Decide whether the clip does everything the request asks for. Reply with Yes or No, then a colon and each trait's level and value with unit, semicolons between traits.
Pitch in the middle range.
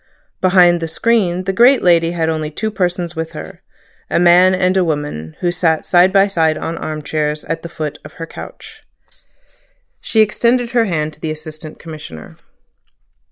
Yes: medium, 170 Hz